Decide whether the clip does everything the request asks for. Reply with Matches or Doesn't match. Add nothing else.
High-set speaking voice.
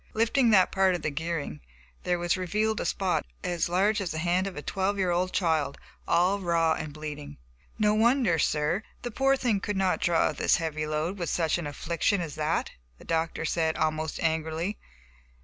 Doesn't match